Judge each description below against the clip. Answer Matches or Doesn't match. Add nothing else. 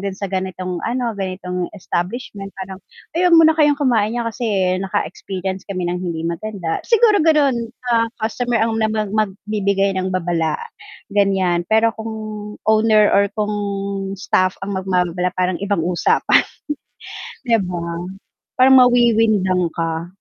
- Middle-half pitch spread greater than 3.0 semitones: Matches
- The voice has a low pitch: Doesn't match